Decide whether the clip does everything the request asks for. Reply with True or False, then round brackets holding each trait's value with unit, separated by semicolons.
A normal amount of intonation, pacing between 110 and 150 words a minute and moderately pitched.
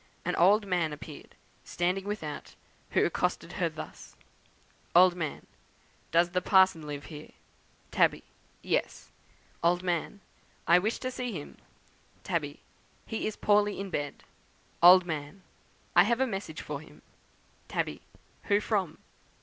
True (4.1 semitones; 135 wpm; 180 Hz)